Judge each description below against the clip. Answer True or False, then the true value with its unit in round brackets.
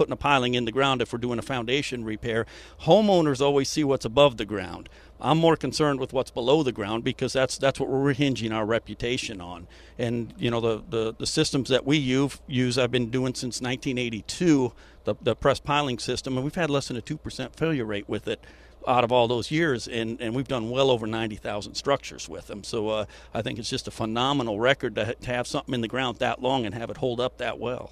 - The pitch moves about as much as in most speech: True (3.1 semitones)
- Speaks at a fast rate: True (230 wpm)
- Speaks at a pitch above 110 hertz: True (125 Hz)